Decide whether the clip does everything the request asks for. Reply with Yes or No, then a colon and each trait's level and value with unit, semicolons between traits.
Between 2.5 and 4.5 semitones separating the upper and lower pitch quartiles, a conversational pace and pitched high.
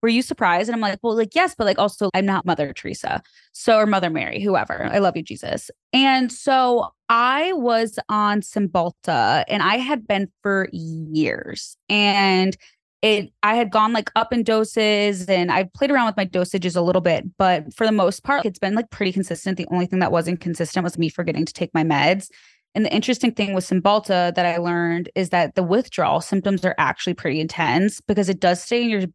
No: average, 3.9 semitones; fast, 210 wpm; high, 195 Hz